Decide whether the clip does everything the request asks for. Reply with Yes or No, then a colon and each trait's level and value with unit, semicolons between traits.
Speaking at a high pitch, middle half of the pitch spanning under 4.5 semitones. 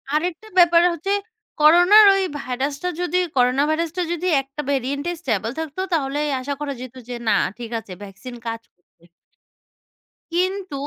No: very high, 285 Hz; average, 5.3 semitones